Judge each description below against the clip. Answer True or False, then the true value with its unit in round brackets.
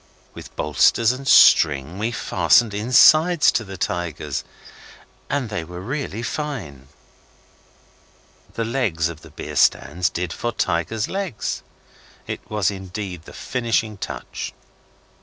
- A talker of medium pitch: False (100 Hz)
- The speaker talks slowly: True (120 wpm)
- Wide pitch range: True (6.0 semitones)